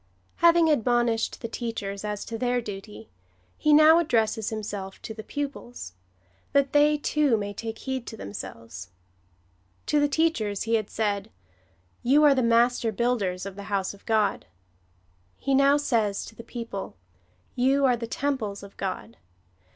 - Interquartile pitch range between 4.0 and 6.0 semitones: Yes, average, 5.1 semitones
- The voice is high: Yes, high, 225 Hz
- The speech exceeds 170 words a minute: No, average, 165 wpm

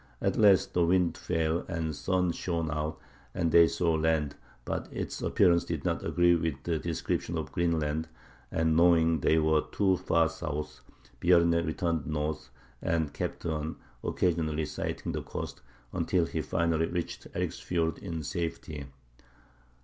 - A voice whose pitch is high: No, very low, 80 Hz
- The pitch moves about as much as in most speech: No, narrow, 1.5 semitones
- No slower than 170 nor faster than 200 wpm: No, average, 145 wpm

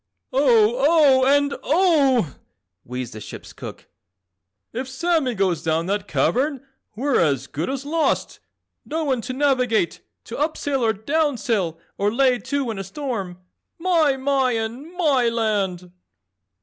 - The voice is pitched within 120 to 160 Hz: No, very high, 255 Hz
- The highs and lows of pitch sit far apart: Yes, wide, 5.7 semitones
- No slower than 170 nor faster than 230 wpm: No, average, 140 wpm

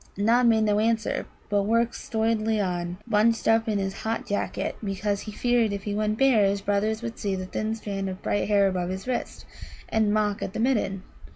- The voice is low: No, high, 210 Hz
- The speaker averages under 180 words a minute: No, fast, 205 wpm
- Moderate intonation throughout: No, narrow, 2.1 semitones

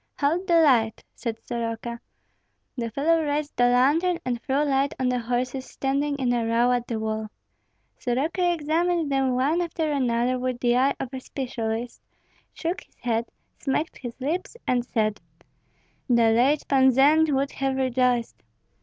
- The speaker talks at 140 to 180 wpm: Yes, average, 160 wpm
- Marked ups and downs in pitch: No, average, 3.4 semitones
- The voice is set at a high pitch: Yes, very high, 260 Hz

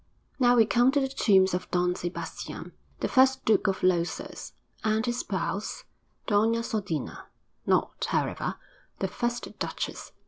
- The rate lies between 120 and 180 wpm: Yes, average, 140 wpm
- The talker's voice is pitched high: Yes, high, 215 Hz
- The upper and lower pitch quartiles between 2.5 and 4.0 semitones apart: No, average, 4.4 semitones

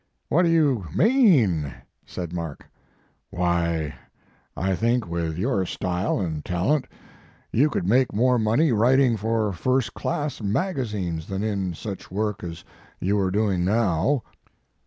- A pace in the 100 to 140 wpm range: Yes, slow, 135 wpm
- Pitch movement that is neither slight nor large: No, wide, 6.1 semitones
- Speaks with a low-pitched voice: Yes, low, 105 Hz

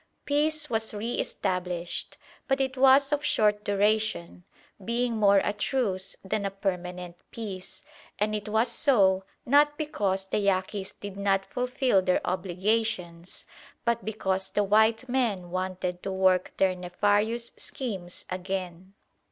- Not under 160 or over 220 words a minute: No, slow, 135 wpm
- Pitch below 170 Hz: No, high, 200 Hz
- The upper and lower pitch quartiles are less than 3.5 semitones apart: No, average, 3.9 semitones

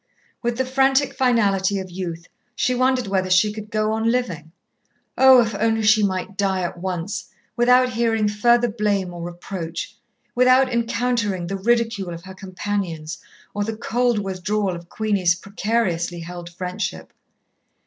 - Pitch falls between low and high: No, high, 205 Hz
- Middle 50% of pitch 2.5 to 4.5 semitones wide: Yes, average, 4.2 semitones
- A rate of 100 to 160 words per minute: Yes, average, 150 wpm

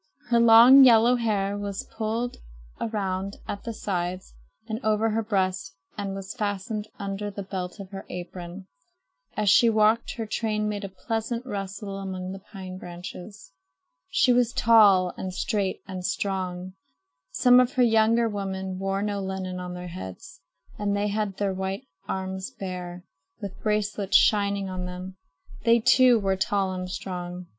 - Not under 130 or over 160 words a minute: Yes, average, 155 wpm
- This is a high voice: Yes, high, 200 Hz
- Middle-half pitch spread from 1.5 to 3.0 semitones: Yes, average, 2.7 semitones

